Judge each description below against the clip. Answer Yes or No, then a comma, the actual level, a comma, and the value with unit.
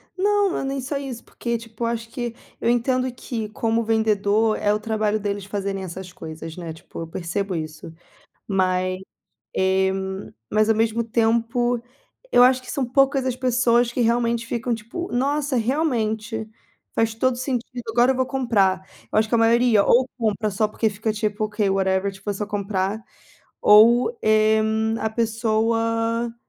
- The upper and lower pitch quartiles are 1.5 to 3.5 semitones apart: Yes, average, 2.8 semitones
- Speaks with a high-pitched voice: Yes, high, 225 Hz